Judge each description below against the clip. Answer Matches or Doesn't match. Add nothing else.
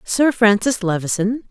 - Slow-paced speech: Matches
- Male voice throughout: Doesn't match